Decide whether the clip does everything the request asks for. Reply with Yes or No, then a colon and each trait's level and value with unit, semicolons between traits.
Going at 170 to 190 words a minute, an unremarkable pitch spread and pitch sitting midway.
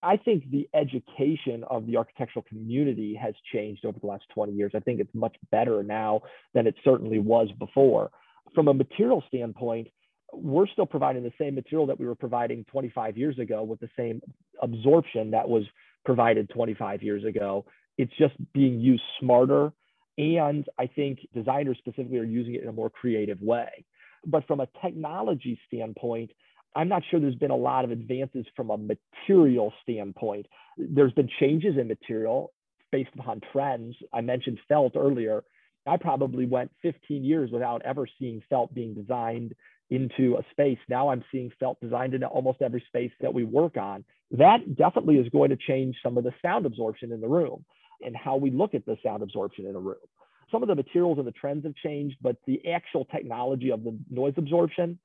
No: average, 185 wpm; average, 3.8 semitones; low, 130 Hz